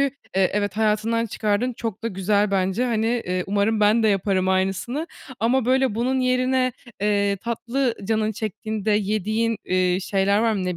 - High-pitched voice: Yes, high, 215 Hz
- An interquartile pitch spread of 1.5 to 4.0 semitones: Yes, average, 2.8 semitones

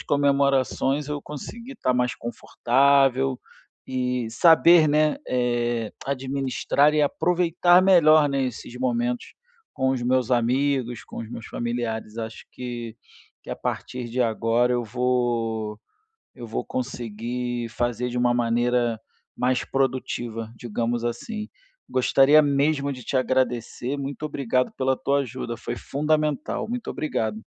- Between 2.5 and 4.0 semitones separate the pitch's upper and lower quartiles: Yes, average, 2.8 semitones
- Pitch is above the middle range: No, low, 125 Hz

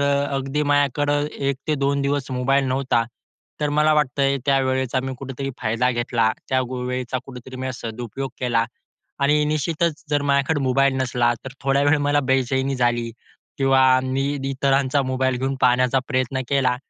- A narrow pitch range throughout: Yes, narrow, 1.7 semitones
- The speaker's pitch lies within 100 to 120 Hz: No, low, 135 Hz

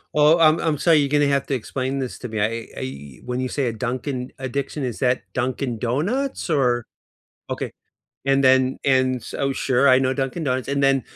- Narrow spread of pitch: Yes, narrow, 2.0 semitones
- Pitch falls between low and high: No, low, 130 Hz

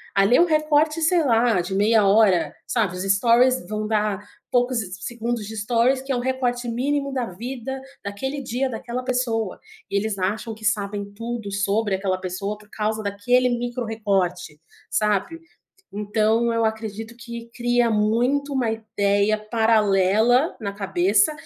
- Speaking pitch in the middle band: No, high, 220 Hz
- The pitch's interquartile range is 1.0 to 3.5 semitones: Yes, average, 3.2 semitones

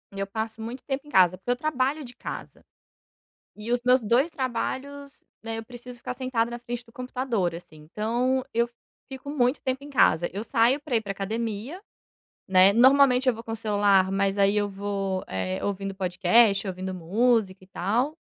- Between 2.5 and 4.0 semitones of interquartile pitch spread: No, average, 4.4 semitones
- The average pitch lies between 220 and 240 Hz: Yes, high, 230 Hz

